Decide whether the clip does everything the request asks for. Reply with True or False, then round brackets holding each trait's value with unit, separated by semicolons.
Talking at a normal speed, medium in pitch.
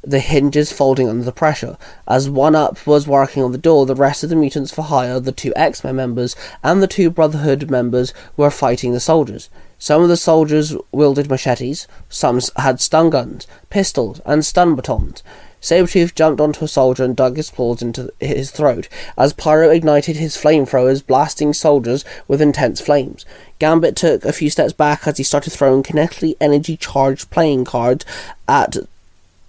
True (175 wpm; 145 Hz)